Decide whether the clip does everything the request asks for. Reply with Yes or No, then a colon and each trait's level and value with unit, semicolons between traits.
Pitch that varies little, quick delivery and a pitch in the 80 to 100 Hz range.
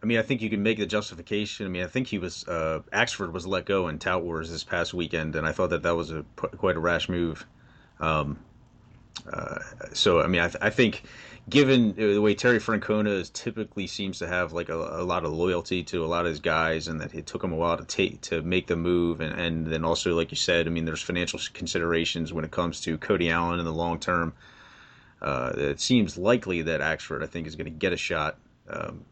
No: average, 3.3 semitones; fast, 245 wpm; very low, 85 Hz